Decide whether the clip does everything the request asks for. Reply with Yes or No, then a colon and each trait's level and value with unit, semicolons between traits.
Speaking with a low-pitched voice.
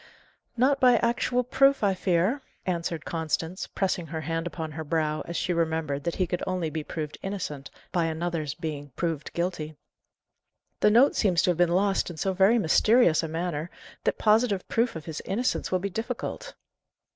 No: medium, 175 Hz